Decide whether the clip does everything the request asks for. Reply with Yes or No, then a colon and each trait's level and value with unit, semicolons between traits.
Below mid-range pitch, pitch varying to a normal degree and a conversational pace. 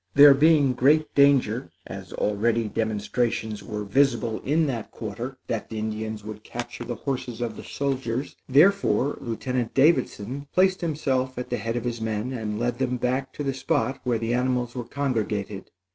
Yes: low, 125 Hz; average, 3.6 semitones; average, 170 wpm